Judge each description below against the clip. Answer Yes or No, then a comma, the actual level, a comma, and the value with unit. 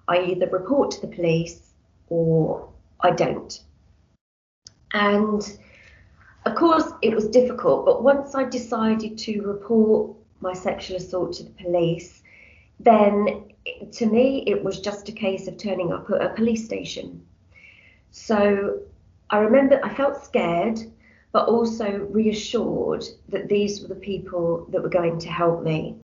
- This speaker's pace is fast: No, average, 145 wpm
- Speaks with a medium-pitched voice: No, high, 200 Hz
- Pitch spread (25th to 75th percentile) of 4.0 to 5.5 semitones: Yes, average, 4.6 semitones